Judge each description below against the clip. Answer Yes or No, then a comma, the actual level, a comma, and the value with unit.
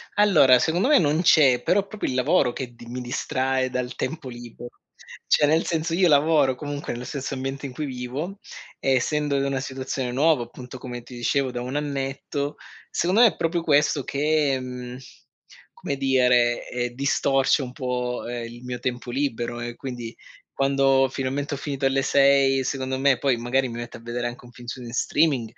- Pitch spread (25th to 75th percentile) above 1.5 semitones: Yes, narrow, 2.6 semitones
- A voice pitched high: No, low, 135 Hz